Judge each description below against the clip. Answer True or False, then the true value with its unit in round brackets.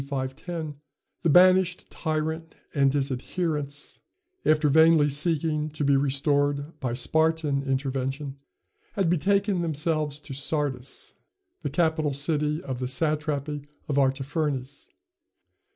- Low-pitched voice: False (150 Hz)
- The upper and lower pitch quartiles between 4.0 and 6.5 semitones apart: False (2.5 semitones)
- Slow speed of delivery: True (110 wpm)